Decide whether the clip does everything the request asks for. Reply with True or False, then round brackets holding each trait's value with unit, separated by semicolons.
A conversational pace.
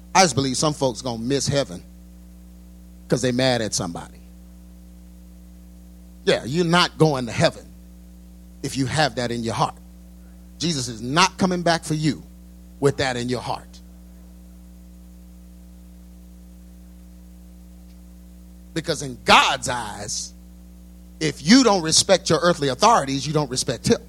False (130 wpm)